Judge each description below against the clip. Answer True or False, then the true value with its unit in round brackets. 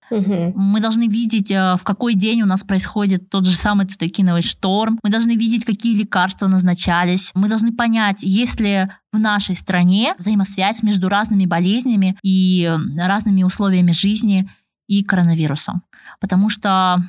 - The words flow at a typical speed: True (140 wpm)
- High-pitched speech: True (195 Hz)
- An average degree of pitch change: False (2.2 semitones)